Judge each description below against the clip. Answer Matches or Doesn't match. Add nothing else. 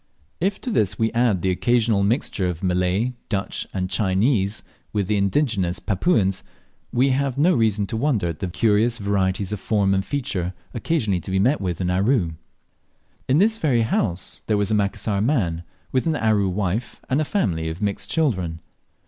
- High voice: Doesn't match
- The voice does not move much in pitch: Doesn't match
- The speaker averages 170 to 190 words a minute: Matches